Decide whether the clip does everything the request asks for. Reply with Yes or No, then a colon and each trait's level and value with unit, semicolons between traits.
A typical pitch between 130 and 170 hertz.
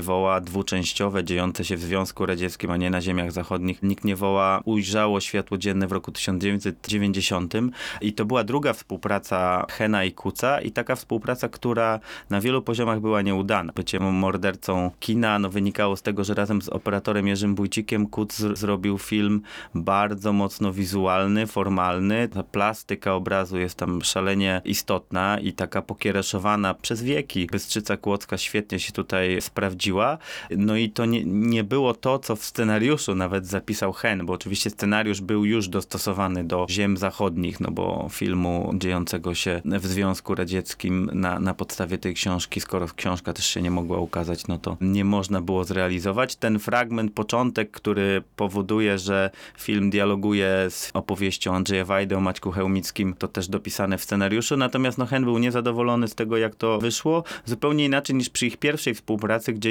No: low, 100 Hz